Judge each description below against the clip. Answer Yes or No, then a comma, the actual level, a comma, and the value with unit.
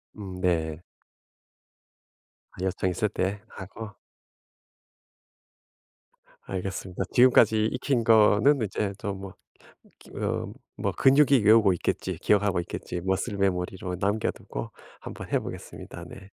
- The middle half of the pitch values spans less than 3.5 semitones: Yes, average, 2.9 semitones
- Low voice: Yes, low, 100 Hz